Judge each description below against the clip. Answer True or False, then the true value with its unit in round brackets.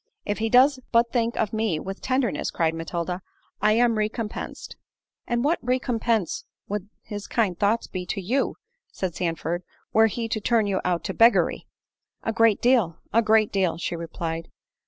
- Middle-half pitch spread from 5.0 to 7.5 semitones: False (4.4 semitones)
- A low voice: False (215 Hz)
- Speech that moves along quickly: False (165 wpm)